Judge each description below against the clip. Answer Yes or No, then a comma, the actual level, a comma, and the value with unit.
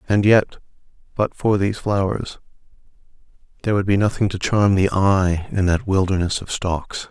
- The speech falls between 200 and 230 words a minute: No, average, 160 wpm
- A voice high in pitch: No, low, 100 Hz